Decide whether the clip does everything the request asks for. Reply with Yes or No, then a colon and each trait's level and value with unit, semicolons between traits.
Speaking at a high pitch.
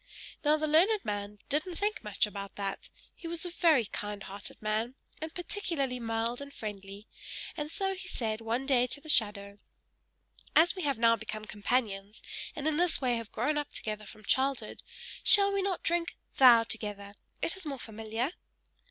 Yes: high, 245 Hz